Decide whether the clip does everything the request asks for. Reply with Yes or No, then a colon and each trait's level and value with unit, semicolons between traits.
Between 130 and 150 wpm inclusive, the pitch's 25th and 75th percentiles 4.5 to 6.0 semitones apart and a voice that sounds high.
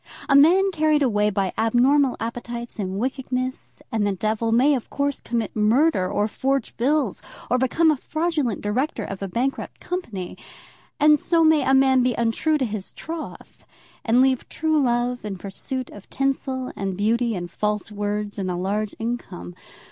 No: average, 170 wpm; average, 4.8 semitones; high, 240 Hz